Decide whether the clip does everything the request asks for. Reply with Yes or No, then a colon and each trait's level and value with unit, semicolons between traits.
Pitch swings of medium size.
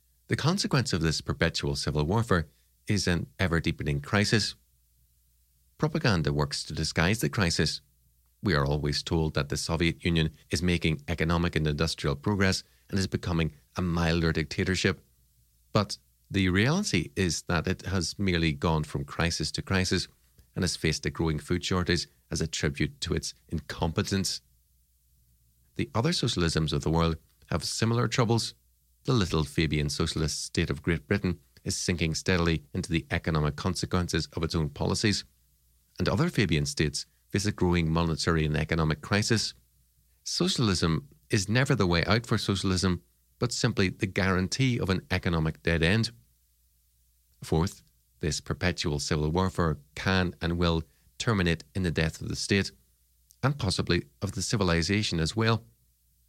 Yes: average, 4.7 semitones